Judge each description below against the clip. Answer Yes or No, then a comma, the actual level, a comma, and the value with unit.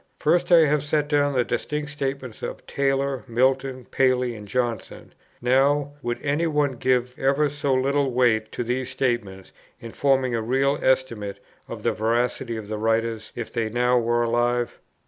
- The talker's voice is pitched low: Yes, low, 130 Hz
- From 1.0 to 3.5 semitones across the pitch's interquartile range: Yes, average, 2.9 semitones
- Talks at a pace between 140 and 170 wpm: Yes, average, 165 wpm